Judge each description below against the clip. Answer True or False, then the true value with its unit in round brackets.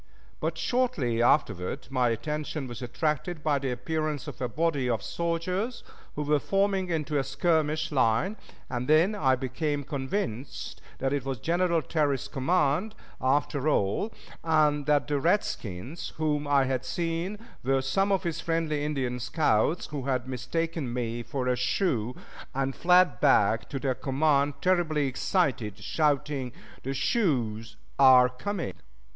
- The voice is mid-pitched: True (145 Hz)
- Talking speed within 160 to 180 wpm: False (145 wpm)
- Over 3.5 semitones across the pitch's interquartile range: True (4.3 semitones)